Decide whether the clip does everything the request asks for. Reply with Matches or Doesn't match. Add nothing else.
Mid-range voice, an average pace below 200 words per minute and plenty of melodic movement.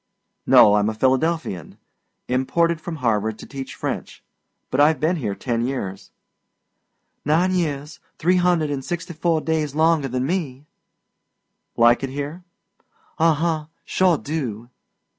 Doesn't match